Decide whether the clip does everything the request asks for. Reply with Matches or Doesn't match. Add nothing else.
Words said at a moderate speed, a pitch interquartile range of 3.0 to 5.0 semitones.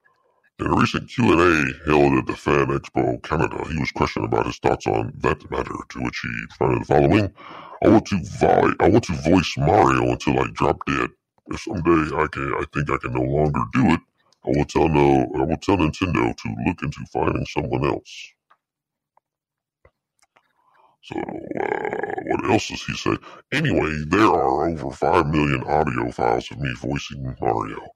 Matches